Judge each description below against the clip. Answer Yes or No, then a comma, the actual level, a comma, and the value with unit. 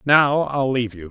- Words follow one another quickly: Yes, fast, 215 wpm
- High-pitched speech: No, low, 130 Hz